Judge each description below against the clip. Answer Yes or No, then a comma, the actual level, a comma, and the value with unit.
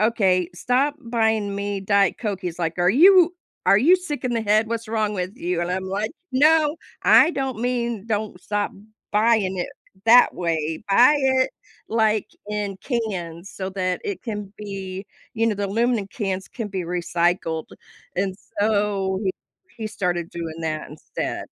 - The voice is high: Yes, high, 205 Hz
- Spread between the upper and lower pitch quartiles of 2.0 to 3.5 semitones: No, average, 3.9 semitones